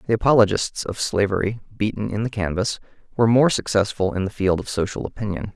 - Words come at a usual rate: Yes, average, 185 wpm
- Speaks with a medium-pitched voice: No, low, 105 Hz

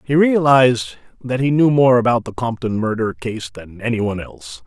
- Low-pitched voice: Yes, low, 120 Hz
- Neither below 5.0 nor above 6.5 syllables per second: Yes, 5.5 syllables/s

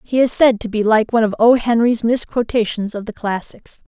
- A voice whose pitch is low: No, high, 225 Hz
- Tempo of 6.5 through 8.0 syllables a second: No, 5.4 syllables/s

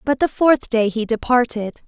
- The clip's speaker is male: No, female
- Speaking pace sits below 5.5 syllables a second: Yes, 4.9 syllables/s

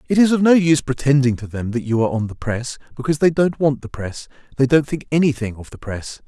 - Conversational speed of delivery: No, fast, 260 wpm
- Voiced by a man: Yes, male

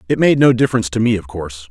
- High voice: No, low, 125 Hz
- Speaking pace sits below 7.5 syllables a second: No, 8.0 syllables/s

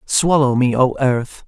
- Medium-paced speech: Yes, average, 165 wpm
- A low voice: Yes, low, 130 Hz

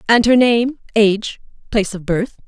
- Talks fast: No, average, 170 wpm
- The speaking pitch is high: Yes, high, 220 Hz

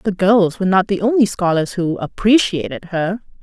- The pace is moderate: Yes, average, 175 wpm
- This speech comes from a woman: Yes, female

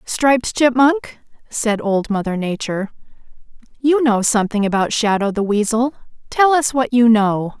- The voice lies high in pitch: Yes, high, 230 Hz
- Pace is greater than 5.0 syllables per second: No, 4.7 syllables/s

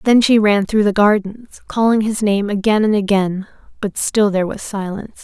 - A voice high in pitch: Yes, high, 205 Hz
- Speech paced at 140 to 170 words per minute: No, average, 195 wpm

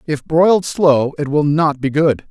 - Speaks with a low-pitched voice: No, medium, 150 Hz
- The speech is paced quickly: Yes, fast, 210 wpm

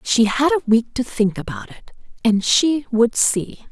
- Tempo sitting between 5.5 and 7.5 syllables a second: No, 4.2 syllables/s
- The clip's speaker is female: Yes, female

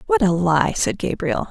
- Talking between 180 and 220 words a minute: Yes, average, 200 wpm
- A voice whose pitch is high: No, medium, 170 Hz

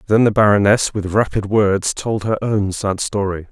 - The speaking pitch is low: Yes, low, 105 Hz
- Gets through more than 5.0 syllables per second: No, 4.6 syllables/s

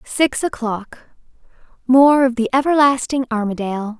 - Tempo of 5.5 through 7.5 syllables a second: No, 5.0 syllables/s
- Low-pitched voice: No, very high, 250 Hz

